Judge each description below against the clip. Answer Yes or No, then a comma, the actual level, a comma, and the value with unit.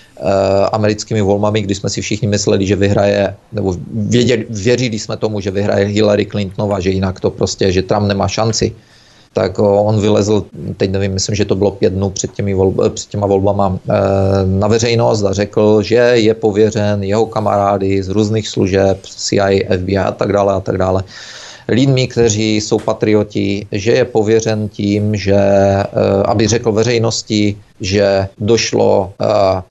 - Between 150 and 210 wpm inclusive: Yes, average, 155 wpm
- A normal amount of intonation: No, narrow, 1.8 semitones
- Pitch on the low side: Yes, low, 105 Hz